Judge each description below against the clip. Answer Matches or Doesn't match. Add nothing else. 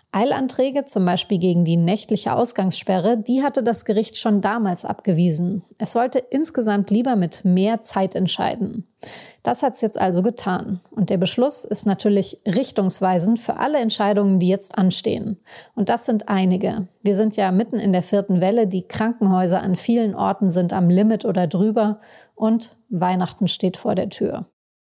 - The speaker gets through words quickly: Doesn't match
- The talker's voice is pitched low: Doesn't match